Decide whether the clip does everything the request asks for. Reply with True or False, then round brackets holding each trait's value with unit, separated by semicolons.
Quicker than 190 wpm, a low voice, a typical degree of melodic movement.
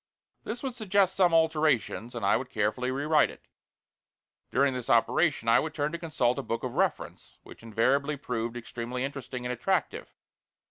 False (170 wpm; 130 Hz; 4.9 semitones)